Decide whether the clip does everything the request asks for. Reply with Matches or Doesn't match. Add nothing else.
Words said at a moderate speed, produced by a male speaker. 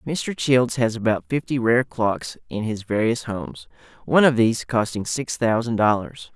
Matches